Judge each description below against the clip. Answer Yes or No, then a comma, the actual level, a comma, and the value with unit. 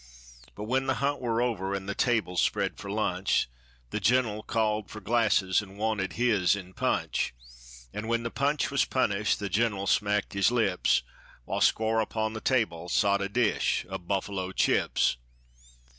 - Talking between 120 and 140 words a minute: No, average, 165 wpm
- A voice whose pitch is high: No, low, 105 Hz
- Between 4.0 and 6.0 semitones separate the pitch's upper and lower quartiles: No, average, 2.9 semitones